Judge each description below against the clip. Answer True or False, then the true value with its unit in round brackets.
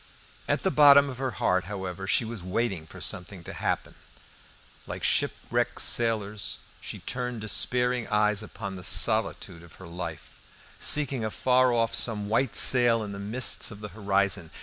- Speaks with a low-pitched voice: True (105 Hz)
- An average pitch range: True (4.1 semitones)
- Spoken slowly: False (160 wpm)